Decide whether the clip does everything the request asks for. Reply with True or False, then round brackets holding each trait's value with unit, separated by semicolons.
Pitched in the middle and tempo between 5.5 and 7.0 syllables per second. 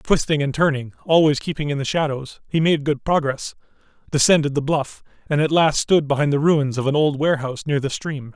True (145 Hz; 5.7 syllables/s)